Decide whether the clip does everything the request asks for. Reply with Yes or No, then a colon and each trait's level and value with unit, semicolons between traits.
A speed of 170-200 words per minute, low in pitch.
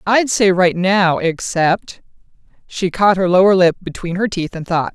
No: average, 180 wpm; medium, 185 Hz